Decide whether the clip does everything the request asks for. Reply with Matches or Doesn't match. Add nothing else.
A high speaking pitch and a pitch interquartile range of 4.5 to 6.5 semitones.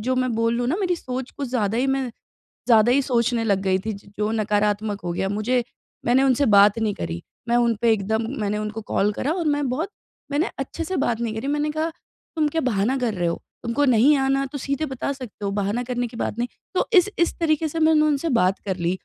Matches